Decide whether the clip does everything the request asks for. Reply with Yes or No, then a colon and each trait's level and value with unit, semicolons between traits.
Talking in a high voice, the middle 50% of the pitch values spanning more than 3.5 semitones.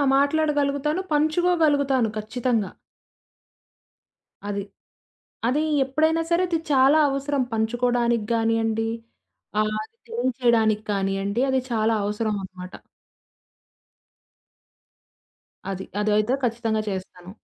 Yes: high, 235 Hz; average, 4.9 semitones